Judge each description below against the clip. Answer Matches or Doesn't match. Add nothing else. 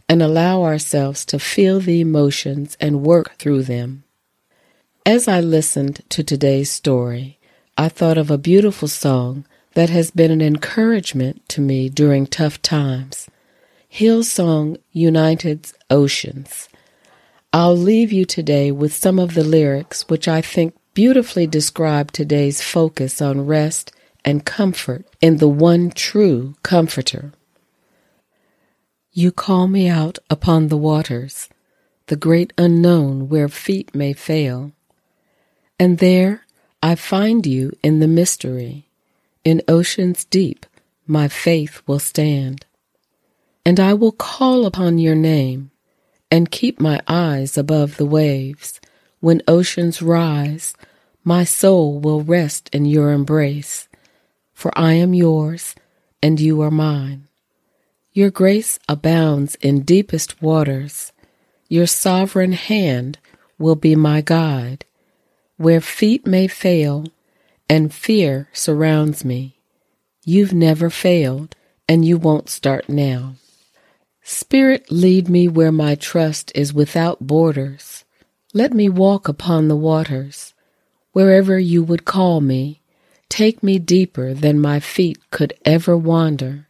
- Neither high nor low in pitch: Matches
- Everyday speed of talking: Doesn't match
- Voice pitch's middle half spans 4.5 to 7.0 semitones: Doesn't match